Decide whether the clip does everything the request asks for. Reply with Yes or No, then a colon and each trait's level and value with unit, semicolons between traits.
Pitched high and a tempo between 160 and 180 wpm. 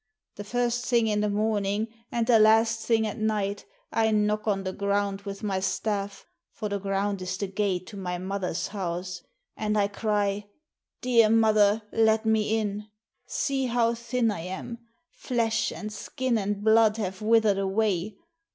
Yes: high, 210 Hz; average, 170 wpm